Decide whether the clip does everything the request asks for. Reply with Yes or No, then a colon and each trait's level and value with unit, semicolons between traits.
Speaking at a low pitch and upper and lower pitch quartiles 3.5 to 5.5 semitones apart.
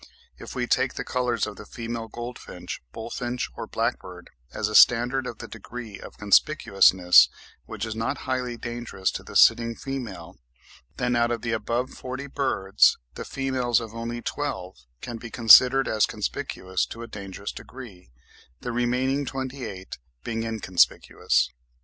No: low, 120 Hz; average, 2.7 semitones